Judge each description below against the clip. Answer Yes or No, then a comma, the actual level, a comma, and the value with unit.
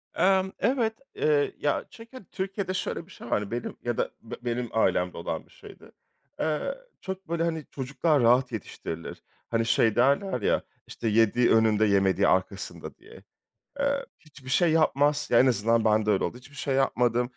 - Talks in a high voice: No, low, 130 Hz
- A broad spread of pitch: Yes, wide, 6.5 semitones